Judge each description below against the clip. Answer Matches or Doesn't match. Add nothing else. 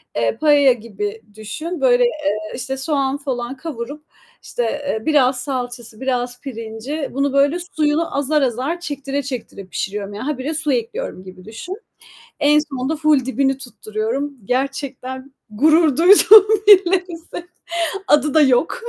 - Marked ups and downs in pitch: Doesn't match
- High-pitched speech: Matches